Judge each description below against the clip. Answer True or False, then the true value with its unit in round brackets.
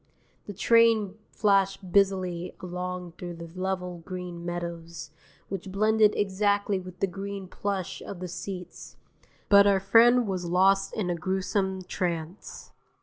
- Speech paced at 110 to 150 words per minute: True (135 wpm)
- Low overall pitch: False (190 Hz)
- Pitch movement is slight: True (2.1 semitones)